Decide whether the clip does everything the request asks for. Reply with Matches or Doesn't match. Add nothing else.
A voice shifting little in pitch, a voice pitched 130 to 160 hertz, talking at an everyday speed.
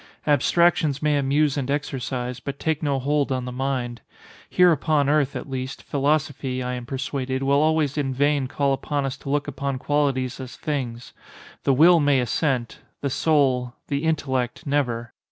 Matches